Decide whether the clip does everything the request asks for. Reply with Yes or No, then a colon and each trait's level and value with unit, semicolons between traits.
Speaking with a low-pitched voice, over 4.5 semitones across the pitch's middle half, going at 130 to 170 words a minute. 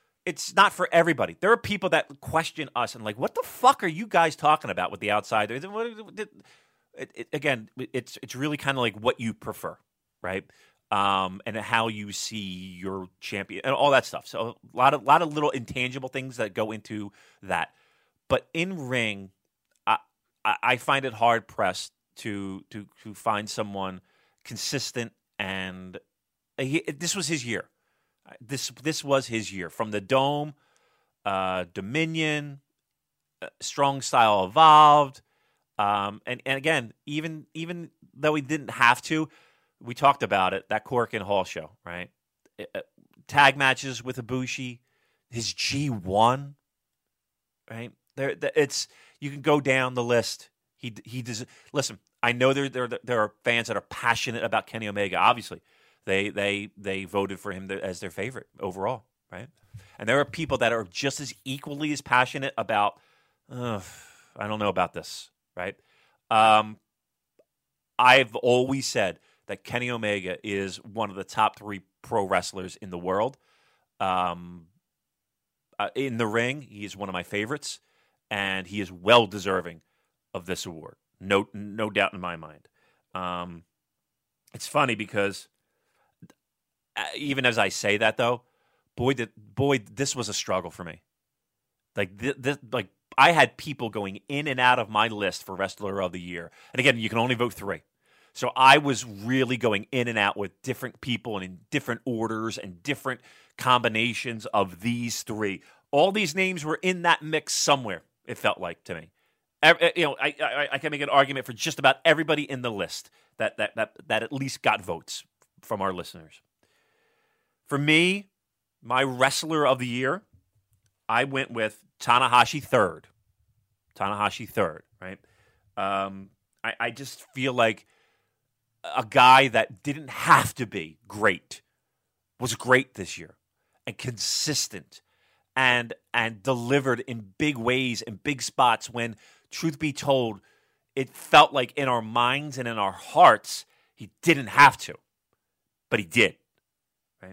Yes: low, 120 Hz; average, 5.1 semitones; average, 160 wpm